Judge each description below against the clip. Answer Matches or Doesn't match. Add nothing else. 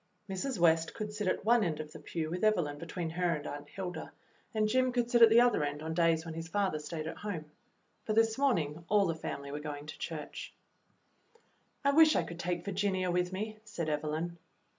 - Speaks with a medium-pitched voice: Matches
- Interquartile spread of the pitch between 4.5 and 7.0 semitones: Matches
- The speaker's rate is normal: Doesn't match